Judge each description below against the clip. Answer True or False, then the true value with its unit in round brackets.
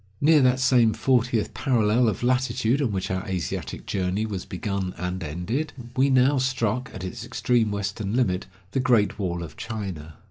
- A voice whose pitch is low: True (110 Hz)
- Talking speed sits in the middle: True (170 wpm)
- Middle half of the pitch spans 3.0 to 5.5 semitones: True (5.1 semitones)